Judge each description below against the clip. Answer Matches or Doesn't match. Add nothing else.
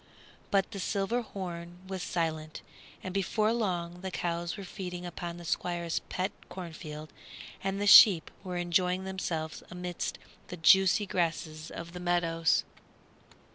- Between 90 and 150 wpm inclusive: Matches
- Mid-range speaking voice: Matches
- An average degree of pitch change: Doesn't match